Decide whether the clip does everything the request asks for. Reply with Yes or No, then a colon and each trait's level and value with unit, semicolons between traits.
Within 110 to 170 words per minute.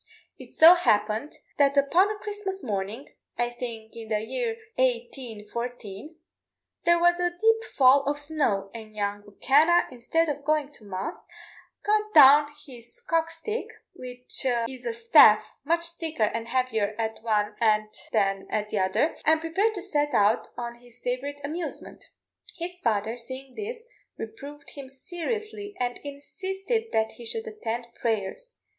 Yes: average, 150 wpm